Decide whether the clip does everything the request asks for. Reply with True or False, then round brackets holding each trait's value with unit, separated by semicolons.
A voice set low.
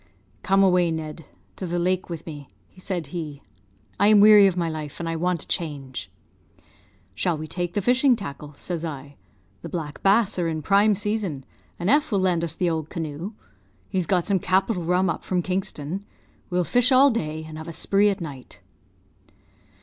False (175 Hz)